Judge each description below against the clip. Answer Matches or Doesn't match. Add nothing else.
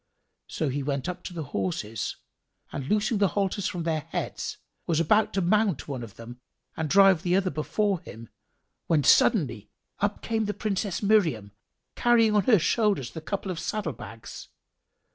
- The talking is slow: Doesn't match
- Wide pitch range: Matches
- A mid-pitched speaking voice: Matches